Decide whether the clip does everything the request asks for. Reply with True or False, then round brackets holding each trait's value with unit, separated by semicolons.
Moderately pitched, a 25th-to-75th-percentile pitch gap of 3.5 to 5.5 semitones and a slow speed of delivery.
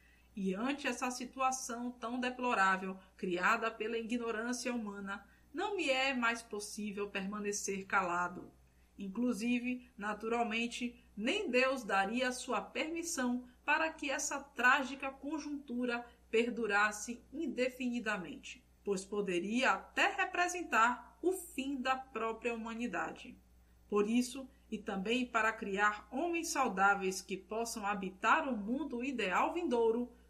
False (235 Hz; 3.9 semitones; 110 wpm)